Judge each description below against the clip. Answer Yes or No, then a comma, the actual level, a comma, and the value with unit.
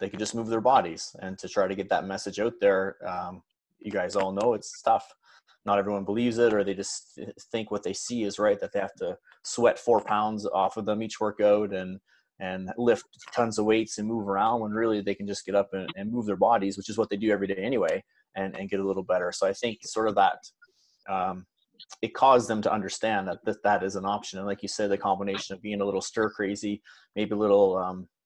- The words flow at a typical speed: No, fast, 250 wpm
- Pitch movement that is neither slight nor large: No, narrow, 2.1 semitones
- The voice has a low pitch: Yes, low, 105 Hz